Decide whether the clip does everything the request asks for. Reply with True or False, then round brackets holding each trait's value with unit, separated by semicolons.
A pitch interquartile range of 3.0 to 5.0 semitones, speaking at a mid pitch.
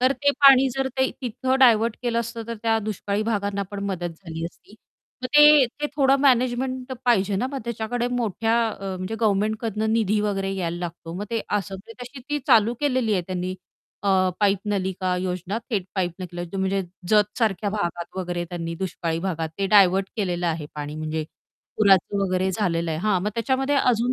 False (4.2 semitones; 205 Hz)